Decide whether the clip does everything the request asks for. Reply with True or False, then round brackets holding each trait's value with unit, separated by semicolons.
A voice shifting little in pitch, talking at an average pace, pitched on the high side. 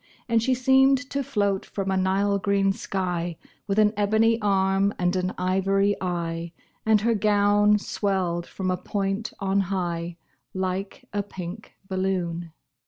True (2.1 semitones; 145 wpm; 195 Hz)